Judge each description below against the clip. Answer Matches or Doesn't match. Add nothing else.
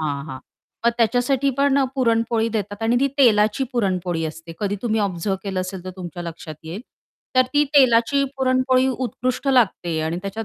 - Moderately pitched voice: Doesn't match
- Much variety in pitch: Matches